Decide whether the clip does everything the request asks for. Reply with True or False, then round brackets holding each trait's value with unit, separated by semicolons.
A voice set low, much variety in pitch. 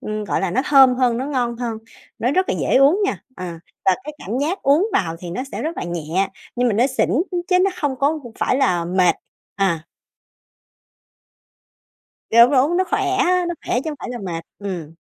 False (250 Hz; 7.9 semitones)